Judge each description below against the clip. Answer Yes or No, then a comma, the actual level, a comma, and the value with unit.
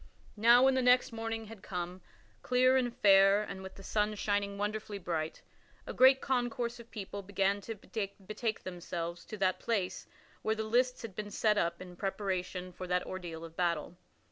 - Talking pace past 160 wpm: Yes, average, 180 wpm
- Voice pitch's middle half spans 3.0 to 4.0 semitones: Yes, average, 3.6 semitones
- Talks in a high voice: Yes, high, 205 Hz